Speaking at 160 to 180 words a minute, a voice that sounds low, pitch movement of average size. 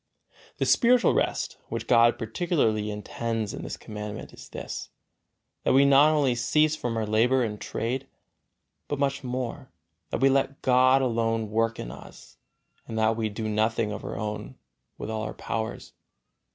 Yes: average, 165 wpm; low, 115 Hz; average, 3.4 semitones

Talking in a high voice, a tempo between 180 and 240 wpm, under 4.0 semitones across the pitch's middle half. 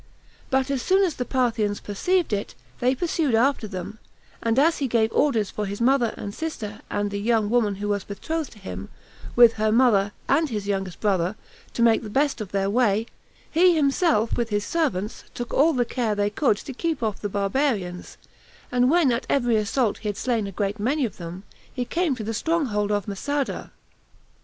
No: high, 230 Hz; average, 200 wpm; average, 4.8 semitones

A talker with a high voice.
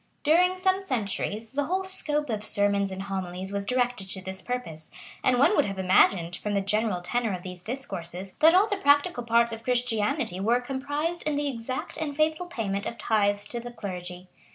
Yes: high, 230 Hz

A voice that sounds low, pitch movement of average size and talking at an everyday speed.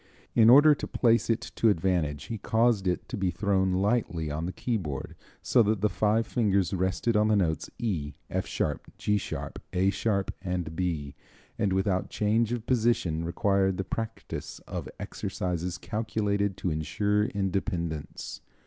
Yes: low, 100 Hz; average, 3.5 semitones; average, 160 wpm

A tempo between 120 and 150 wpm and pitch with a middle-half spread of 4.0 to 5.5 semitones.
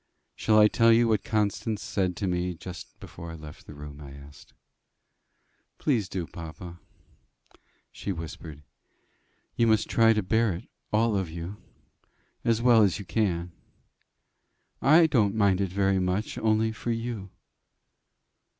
Yes: average, 145 wpm; average, 4.4 semitones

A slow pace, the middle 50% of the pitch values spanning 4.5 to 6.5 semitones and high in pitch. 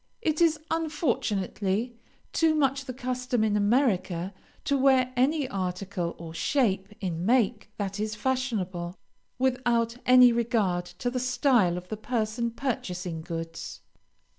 Yes: slow, 130 wpm; average, 5.3 semitones; high, 230 Hz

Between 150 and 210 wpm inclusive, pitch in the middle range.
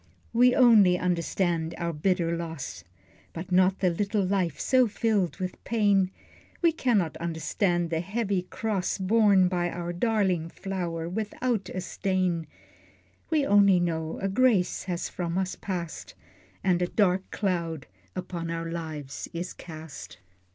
No: slow, 135 wpm; medium, 180 Hz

